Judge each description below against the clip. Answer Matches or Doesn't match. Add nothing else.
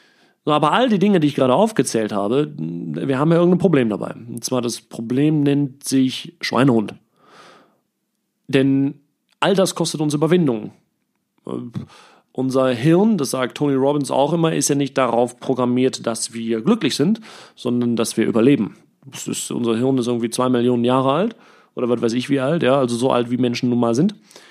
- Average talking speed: Matches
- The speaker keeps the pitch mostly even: Doesn't match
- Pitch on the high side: Doesn't match